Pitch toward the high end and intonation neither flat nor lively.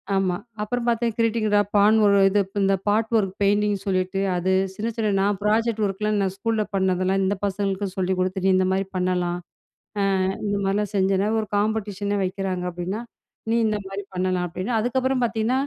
No: high, 200 Hz; narrow, 2.2 semitones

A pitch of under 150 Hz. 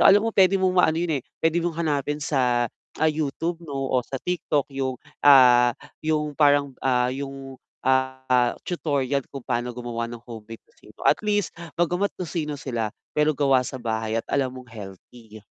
Yes: low, 135 Hz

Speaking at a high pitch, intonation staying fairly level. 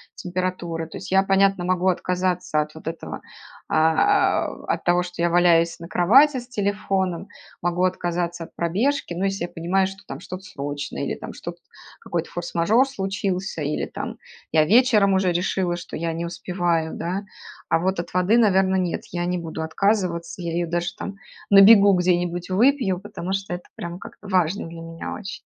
No: medium, 180 Hz; narrow, 2.3 semitones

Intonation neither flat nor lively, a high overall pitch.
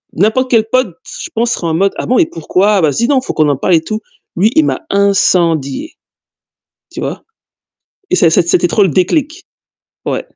No: wide, 6.1 semitones; high, 200 Hz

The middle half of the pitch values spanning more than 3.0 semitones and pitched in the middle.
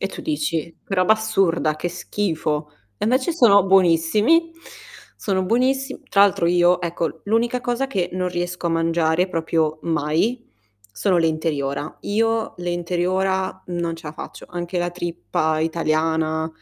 Yes: average, 3.8 semitones; medium, 175 Hz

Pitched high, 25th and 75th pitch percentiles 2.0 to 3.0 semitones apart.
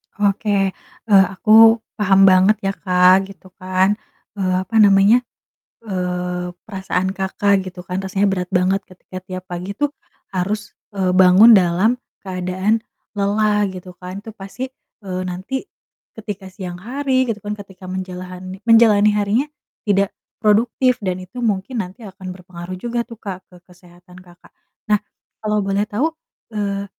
Yes: high, 195 Hz; narrow, 2.4 semitones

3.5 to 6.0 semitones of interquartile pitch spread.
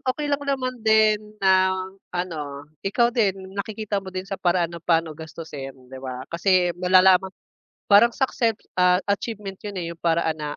Yes: average, 4.0 semitones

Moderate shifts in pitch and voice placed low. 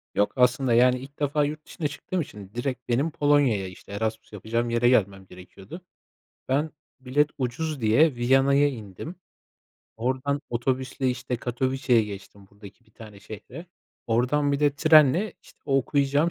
Yes: average, 4.2 semitones; low, 130 Hz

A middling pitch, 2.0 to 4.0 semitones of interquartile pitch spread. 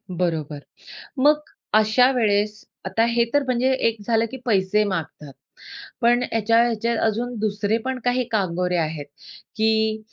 No: high, 220 Hz; average, 3.5 semitones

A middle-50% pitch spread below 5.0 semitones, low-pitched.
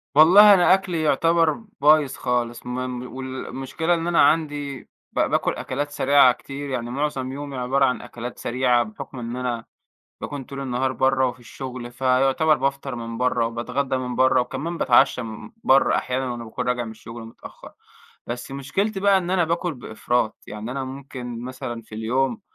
Yes: average, 2.9 semitones; low, 130 Hz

